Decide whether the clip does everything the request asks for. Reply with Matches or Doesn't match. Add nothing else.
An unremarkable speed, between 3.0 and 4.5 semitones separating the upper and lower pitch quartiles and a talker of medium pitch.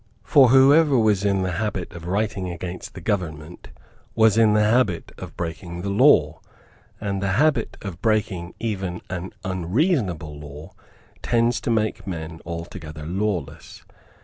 Doesn't match